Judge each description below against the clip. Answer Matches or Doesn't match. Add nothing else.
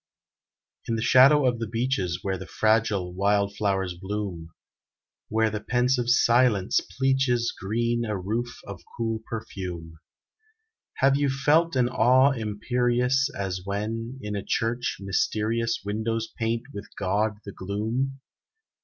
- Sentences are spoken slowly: Matches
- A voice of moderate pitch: Doesn't match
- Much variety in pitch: Doesn't match